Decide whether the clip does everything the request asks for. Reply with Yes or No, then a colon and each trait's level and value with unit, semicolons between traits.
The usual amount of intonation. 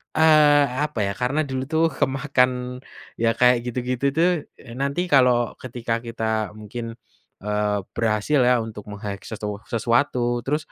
Yes: average, 3.5 semitones